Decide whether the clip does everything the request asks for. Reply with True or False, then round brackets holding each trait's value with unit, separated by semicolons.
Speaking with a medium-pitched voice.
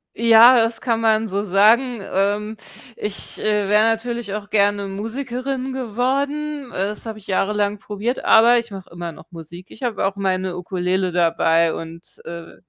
False (210 Hz)